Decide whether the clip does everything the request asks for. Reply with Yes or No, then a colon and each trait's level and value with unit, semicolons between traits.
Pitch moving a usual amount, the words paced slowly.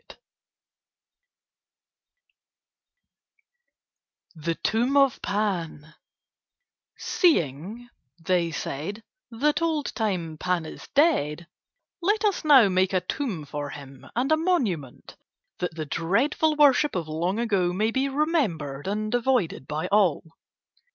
No: wide, 8.8 semitones; slow, 110 wpm